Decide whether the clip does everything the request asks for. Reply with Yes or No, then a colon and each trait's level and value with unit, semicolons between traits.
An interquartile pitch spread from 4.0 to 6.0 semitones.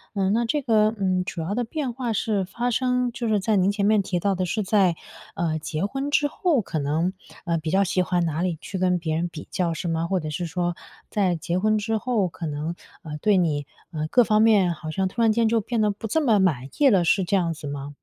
Yes: average, 4.6 semitones